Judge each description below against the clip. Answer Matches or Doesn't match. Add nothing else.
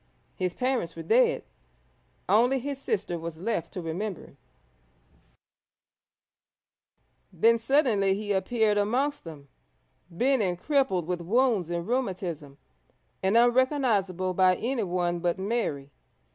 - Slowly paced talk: Matches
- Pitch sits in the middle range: Doesn't match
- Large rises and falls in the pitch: Matches